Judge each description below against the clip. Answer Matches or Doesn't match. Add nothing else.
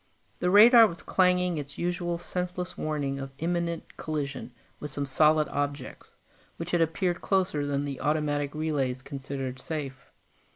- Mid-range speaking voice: Matches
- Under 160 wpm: Matches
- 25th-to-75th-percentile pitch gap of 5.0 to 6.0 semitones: Doesn't match